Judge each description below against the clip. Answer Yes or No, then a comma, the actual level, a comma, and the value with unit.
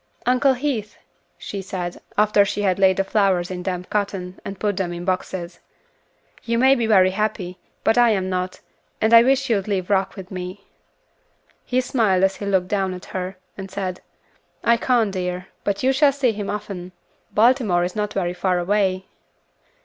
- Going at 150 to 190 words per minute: Yes, average, 185 wpm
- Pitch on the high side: Yes, high, 195 Hz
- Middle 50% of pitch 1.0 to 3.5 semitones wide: Yes, average, 2.9 semitones